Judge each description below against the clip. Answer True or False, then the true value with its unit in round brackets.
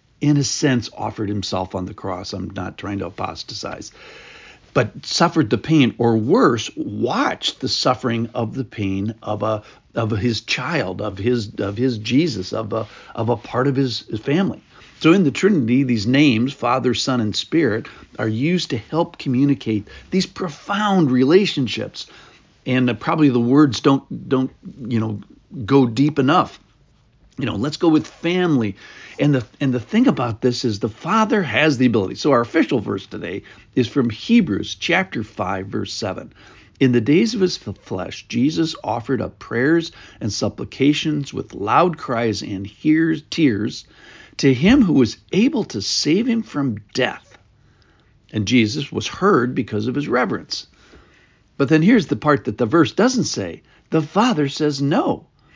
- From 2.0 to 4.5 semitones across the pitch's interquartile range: False (5.6 semitones)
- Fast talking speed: False (165 wpm)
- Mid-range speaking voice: False (130 Hz)